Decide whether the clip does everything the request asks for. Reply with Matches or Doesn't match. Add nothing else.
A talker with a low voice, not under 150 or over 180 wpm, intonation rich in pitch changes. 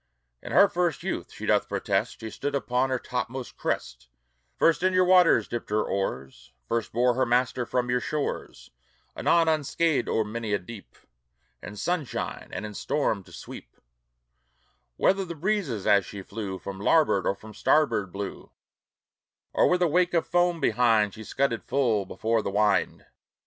Matches